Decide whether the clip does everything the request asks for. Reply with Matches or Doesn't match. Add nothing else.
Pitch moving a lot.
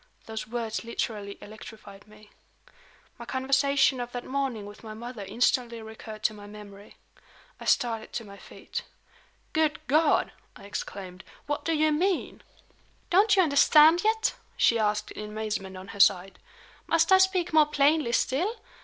Matches